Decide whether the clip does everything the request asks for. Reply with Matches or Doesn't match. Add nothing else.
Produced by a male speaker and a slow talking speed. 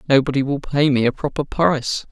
Doesn't match